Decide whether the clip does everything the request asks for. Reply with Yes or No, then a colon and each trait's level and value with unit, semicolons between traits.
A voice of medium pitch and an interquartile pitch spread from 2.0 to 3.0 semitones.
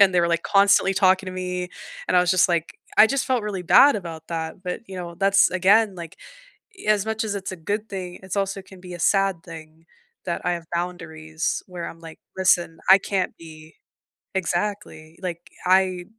Yes: medium, 180 Hz; narrow, 2.6 semitones